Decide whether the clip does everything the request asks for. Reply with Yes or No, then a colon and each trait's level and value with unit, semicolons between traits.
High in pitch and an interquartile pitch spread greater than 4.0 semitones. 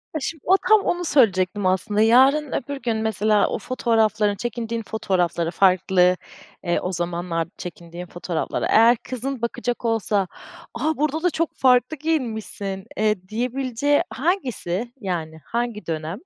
Yes: high, 220 Hz; wide, 5.6 semitones